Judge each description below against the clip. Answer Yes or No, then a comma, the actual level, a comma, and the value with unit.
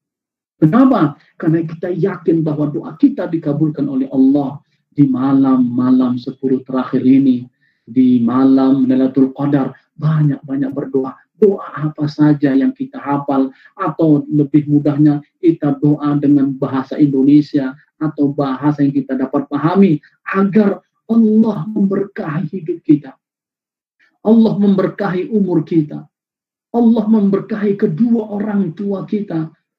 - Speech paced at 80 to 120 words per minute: Yes, average, 115 wpm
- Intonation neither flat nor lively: No, wide, 5.9 semitones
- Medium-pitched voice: Yes, medium, 150 Hz